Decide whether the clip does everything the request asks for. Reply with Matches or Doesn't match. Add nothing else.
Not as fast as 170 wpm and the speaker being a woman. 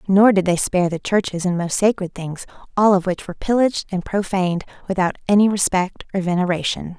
Doesn't match